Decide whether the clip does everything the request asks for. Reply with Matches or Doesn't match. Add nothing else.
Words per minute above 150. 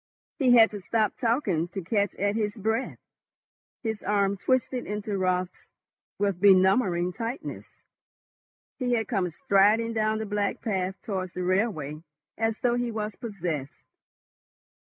Doesn't match